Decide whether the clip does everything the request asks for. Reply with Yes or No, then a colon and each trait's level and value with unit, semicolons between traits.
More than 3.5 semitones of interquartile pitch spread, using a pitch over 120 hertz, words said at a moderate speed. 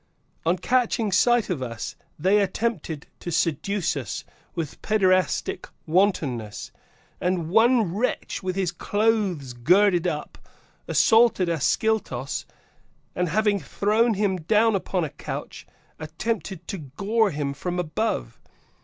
No: average, 5.1 semitones; medium, 185 Hz; slow, 120 wpm